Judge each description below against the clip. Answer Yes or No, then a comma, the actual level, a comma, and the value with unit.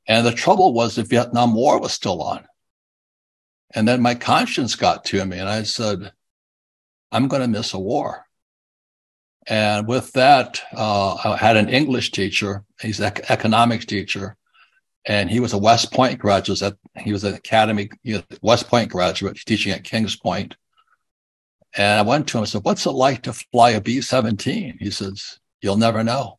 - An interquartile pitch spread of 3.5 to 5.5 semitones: No, average, 2.9 semitones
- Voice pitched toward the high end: No, low, 110 Hz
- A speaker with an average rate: Yes, average, 180 wpm